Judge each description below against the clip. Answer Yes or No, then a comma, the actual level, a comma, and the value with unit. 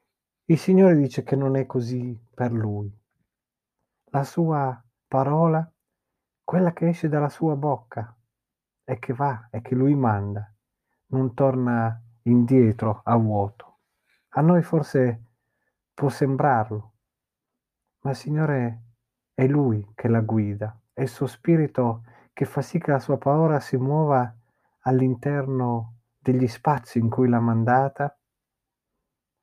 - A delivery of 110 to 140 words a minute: Yes, average, 130 wpm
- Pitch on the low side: Yes, low, 130 Hz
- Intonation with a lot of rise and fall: No, average, 3.5 semitones